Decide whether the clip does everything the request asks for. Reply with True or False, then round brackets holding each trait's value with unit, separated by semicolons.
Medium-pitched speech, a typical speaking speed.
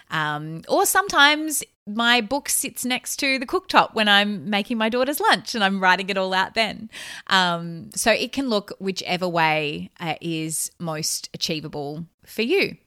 False (200 Hz; 170 wpm)